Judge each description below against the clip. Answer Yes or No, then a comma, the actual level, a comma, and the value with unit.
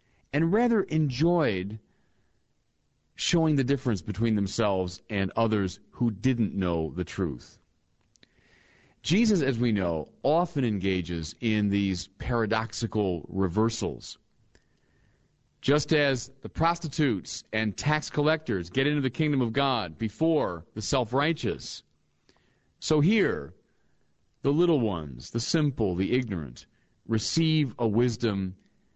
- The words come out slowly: Yes, slow, 110 wpm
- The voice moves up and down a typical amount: No, wide, 6.8 semitones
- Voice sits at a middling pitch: No, low, 115 Hz